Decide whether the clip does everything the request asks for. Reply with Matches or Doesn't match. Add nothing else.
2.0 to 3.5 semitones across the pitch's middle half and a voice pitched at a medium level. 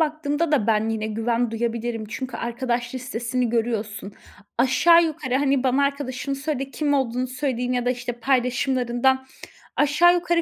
Doesn't match